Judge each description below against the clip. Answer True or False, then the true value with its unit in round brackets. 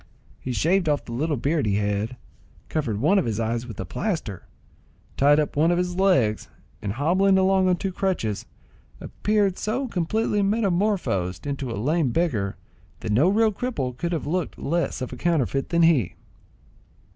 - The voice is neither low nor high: True (160 Hz)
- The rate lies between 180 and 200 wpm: False (170 wpm)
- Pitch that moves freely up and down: True (8.0 semitones)